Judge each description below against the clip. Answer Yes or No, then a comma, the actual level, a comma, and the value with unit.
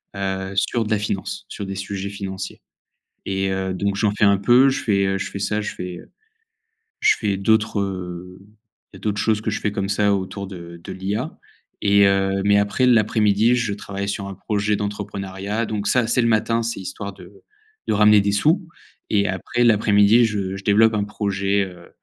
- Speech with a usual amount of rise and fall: No, narrow, 1.6 semitones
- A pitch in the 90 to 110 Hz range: Yes, low, 100 Hz